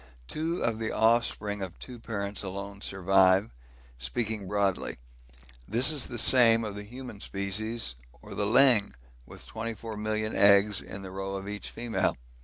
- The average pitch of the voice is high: No, low, 105 Hz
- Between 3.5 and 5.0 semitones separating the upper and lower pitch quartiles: No, average, 2.7 semitones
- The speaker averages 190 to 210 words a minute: No, average, 145 wpm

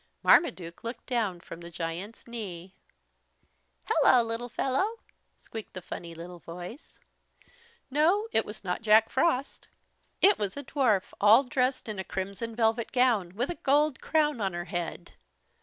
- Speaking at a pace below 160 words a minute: Yes, average, 150 wpm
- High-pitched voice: Yes, high, 225 Hz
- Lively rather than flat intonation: Yes, wide, 6.0 semitones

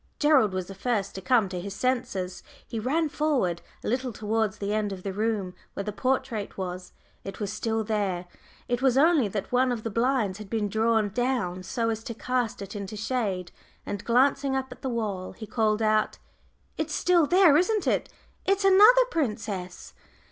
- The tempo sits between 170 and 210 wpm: Yes, average, 190 wpm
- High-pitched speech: Yes, high, 220 Hz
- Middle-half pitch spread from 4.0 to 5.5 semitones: Yes, average, 4.5 semitones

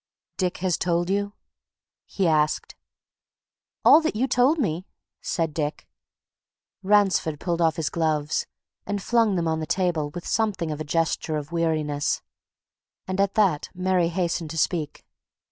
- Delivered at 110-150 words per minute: Yes, average, 145 wpm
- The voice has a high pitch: No, medium, 170 Hz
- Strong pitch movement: No, average, 3.6 semitones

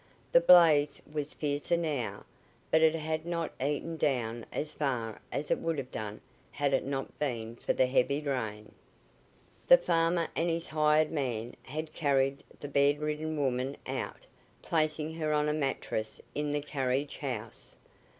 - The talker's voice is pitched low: No, medium, 145 Hz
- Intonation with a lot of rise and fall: No, average, 2.9 semitones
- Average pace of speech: Yes, average, 155 wpm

